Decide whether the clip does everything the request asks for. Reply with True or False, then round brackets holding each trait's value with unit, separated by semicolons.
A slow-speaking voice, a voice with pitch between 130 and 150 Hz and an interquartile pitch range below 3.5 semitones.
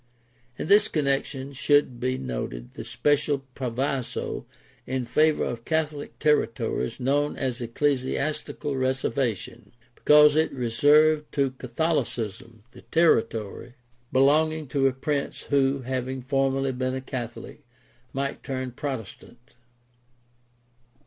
True (110 wpm; 135 Hz; 3.0 semitones)